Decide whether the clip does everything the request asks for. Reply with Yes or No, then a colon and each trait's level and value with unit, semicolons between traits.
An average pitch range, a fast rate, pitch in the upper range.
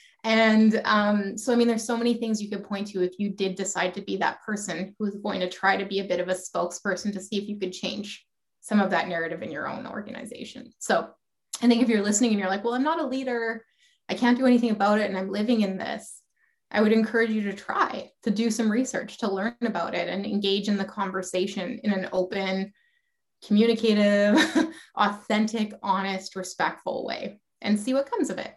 Yes: average, 3.4 semitones; fast, 220 wpm; high, 210 Hz